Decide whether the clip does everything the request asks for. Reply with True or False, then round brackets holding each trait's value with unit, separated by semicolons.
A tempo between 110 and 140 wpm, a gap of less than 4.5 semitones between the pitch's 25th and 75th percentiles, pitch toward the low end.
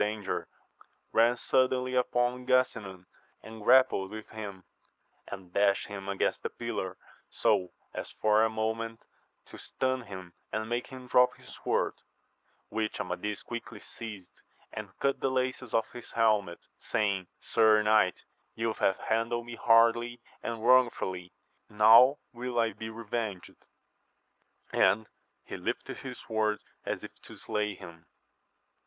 True (135 wpm; 2.8 semitones; 110 Hz)